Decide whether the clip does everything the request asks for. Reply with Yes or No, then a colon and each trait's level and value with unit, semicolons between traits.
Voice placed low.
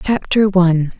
No: medium, 185 Hz